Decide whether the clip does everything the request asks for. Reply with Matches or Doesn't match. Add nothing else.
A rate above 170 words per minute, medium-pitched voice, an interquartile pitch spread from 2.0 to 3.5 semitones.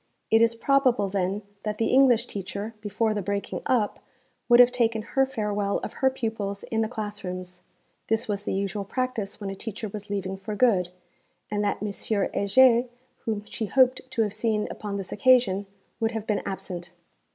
Doesn't match